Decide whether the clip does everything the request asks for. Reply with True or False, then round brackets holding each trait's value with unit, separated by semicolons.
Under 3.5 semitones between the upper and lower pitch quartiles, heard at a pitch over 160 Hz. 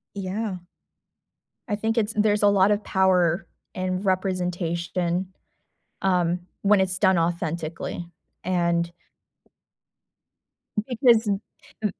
True (2.9 semitones; 185 Hz)